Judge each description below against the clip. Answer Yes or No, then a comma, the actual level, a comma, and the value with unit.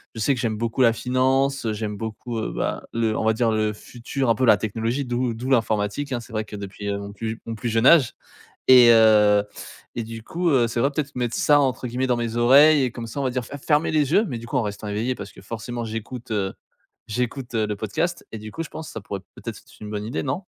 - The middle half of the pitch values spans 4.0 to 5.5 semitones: No, average, 3.0 semitones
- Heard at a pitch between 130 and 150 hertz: No, low, 115 Hz